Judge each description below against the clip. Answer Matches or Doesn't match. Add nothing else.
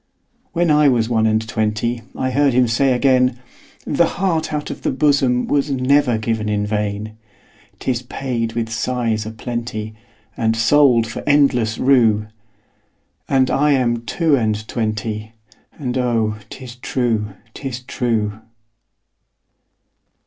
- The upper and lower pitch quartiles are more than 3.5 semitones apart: Doesn't match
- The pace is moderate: Doesn't match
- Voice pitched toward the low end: Matches